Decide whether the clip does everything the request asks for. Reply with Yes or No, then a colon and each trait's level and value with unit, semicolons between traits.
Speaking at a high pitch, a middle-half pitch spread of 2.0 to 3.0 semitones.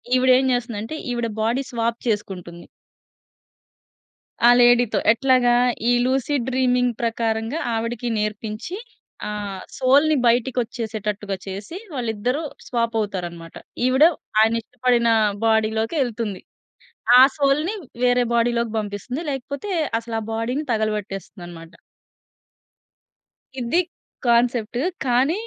Yes: high, 235 Hz; average, 2.7 semitones